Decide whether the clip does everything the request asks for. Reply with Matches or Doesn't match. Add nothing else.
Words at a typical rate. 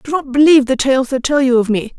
Doesn't match